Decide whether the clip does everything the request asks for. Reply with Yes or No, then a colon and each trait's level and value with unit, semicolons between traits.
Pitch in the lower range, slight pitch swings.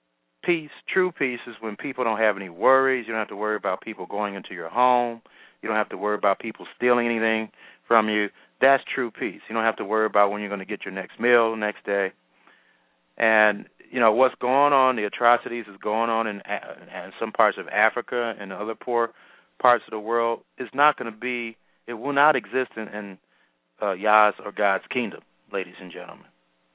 No: low, 110 Hz; average, 3.0 semitones